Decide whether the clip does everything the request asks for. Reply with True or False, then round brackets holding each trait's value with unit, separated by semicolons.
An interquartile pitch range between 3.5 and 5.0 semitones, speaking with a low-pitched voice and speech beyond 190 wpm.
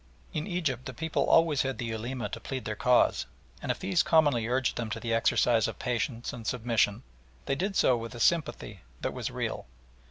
True (4.5 semitones; 125 Hz; 200 wpm)